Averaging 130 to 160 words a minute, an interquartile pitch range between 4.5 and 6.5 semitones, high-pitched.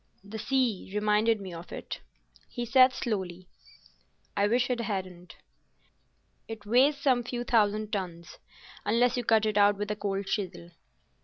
No: average, 145 wpm; average, 3.5 semitones; high, 210 Hz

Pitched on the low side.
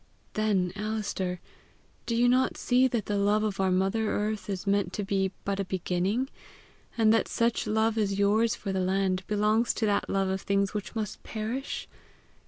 No: high, 205 Hz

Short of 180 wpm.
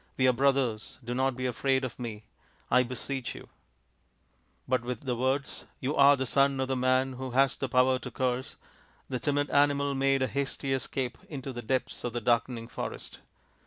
No: average, 195 wpm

